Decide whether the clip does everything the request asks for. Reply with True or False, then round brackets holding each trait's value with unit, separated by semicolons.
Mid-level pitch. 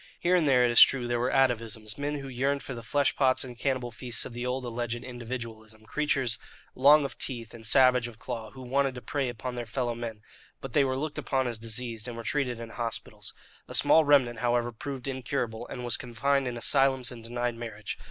False (125 Hz)